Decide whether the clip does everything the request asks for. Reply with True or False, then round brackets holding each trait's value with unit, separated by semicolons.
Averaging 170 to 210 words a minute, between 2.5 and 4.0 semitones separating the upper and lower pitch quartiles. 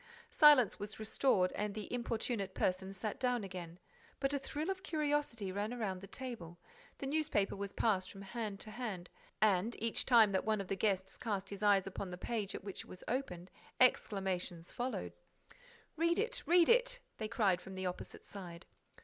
False (185 wpm; 4.7 semitones)